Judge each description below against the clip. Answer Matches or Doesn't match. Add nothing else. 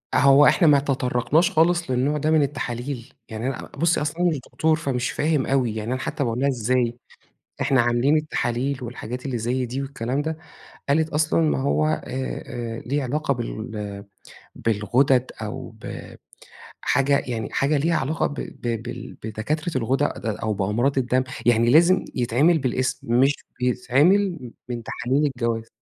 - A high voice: Doesn't match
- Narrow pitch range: Doesn't match